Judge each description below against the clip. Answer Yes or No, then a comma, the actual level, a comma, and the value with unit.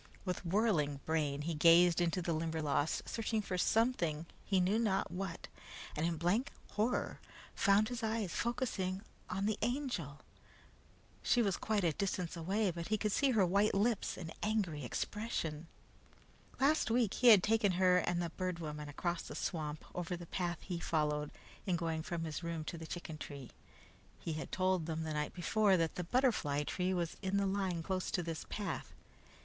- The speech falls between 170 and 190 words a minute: Yes, average, 180 wpm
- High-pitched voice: No, medium, 180 Hz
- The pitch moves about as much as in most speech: Yes, average, 4.2 semitones